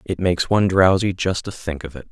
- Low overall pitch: Yes, very low, 90 Hz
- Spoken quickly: Yes, fast, 255 wpm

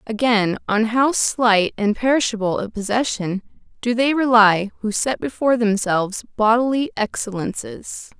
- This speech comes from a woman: Yes, female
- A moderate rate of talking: No, slow, 125 wpm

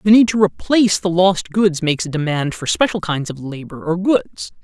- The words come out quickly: Yes, fast, 220 wpm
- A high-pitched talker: No, medium, 170 Hz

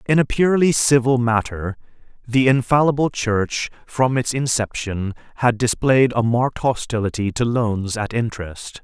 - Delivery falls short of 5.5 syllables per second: Yes, 4.6 syllables/s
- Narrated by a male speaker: Yes, male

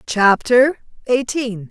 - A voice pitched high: Yes, high, 235 Hz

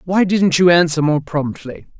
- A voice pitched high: No, medium, 165 Hz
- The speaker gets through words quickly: No, average, 180 wpm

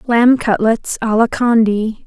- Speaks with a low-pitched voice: No, high, 225 Hz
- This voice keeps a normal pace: Yes, average, 145 wpm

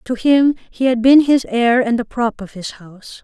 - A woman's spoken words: Yes, female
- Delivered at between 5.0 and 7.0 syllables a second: No, 4.8 syllables/s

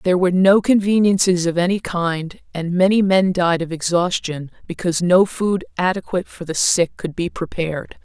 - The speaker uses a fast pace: No, average, 170 wpm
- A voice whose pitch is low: No, medium, 180 Hz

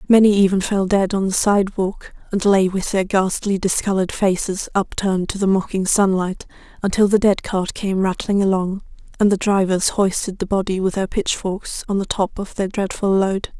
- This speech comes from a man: No, female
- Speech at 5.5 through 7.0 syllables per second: No, 5.1 syllables/s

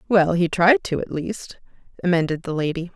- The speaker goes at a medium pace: Yes, average, 185 wpm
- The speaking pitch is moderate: Yes, medium, 175 Hz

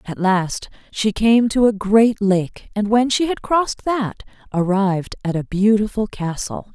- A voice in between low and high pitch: No, high, 210 Hz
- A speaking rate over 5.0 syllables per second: No, 4.2 syllables/s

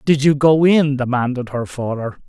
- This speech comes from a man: Yes, male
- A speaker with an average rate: Yes, average, 185 wpm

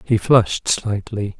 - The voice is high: No, low, 105 Hz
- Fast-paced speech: No, slow, 130 wpm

